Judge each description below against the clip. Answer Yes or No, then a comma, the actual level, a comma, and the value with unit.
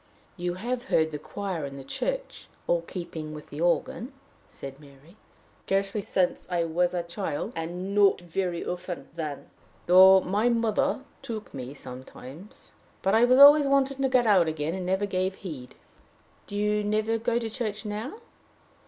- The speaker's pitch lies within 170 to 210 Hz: Yes, high, 190 Hz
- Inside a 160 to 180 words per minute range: Yes, average, 165 wpm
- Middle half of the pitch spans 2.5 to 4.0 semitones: No, average, 4.9 semitones